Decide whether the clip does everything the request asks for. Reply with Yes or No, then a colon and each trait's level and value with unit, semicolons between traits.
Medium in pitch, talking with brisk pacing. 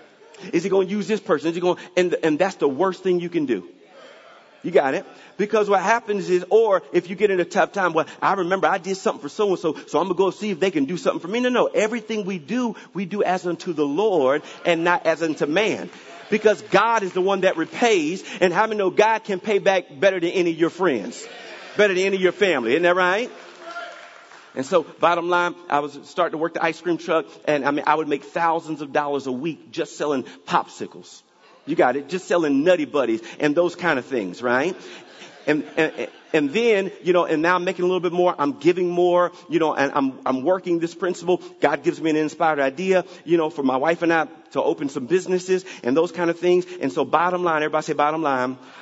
Yes: medium, 175 Hz; fast, 240 wpm